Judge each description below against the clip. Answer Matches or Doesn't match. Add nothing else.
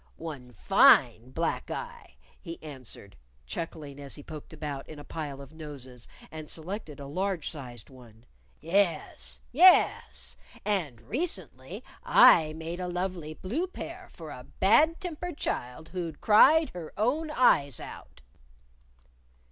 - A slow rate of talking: Matches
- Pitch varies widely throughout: Matches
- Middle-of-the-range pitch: Matches